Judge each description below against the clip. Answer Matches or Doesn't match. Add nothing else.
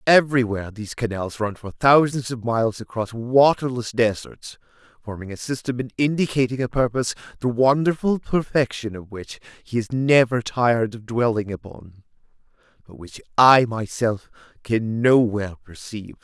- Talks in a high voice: Doesn't match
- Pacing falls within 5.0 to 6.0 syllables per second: Doesn't match